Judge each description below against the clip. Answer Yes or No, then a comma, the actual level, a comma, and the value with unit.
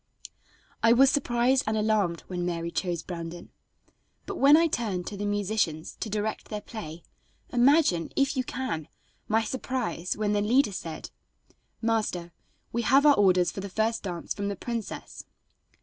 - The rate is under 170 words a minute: Yes, average, 160 wpm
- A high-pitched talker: Yes, high, 210 Hz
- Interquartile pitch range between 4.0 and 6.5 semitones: Yes, average, 5.1 semitones